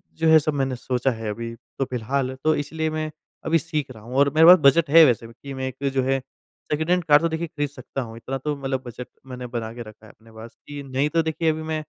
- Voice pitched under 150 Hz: Yes, low, 135 Hz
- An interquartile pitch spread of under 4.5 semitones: Yes, average, 4.0 semitones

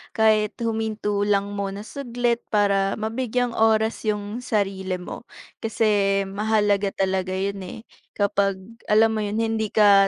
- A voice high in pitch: Yes, high, 210 Hz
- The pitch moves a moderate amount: No, narrow, 1.9 semitones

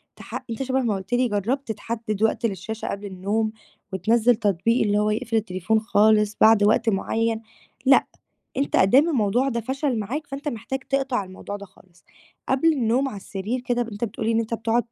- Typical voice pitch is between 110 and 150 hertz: No, high, 225 Hz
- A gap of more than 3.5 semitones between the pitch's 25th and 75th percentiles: No, average, 3.2 semitones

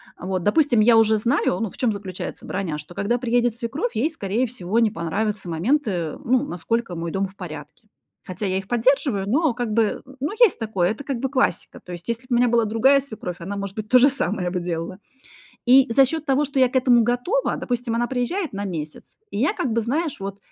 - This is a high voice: Yes, high, 230 Hz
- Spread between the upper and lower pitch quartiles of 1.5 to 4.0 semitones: No, average, 5.0 semitones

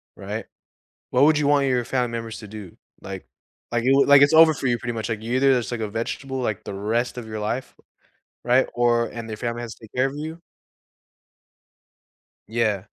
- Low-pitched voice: Yes, low, 120 Hz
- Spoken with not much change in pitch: No, average, 3.0 semitones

